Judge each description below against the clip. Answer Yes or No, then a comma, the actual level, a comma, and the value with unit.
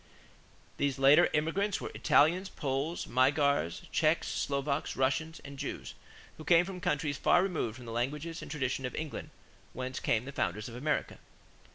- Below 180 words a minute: Yes, average, 165 wpm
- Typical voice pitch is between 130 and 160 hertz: Yes, medium, 140 Hz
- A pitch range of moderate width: Yes, average, 3.5 semitones